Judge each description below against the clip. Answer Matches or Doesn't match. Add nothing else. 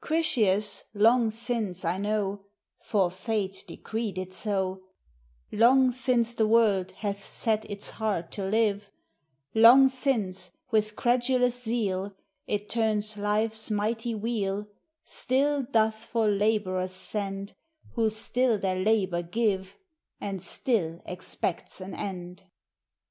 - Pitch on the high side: Matches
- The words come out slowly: Matches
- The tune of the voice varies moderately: Matches